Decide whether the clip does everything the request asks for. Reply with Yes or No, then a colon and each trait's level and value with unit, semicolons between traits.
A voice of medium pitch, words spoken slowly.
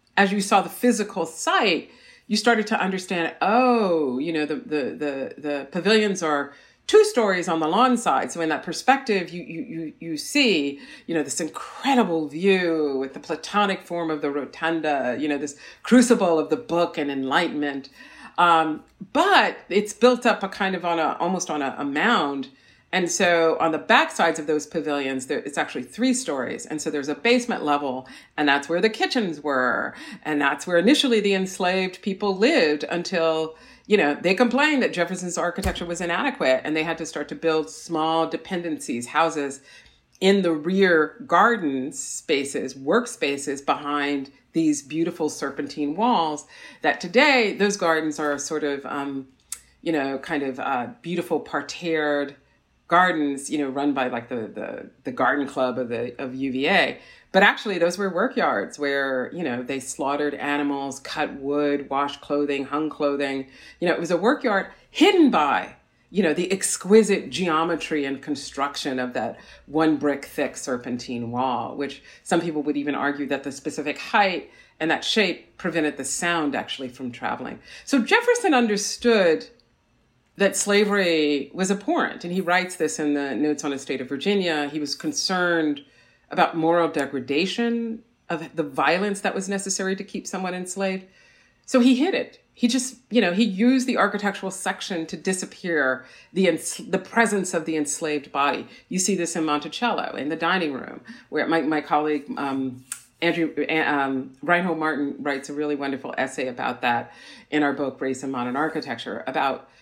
No: medium, 160 Hz; average, 170 wpm